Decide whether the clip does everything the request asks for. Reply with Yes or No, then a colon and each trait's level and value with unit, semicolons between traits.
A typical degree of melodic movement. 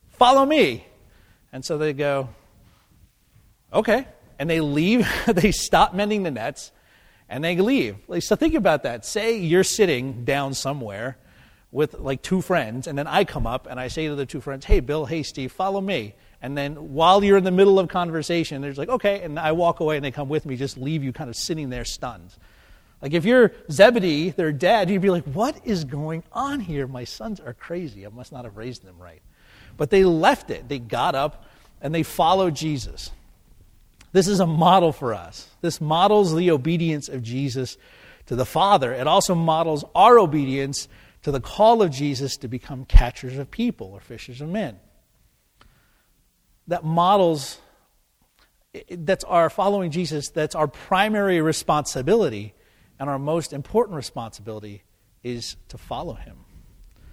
No: wide, 6.2 semitones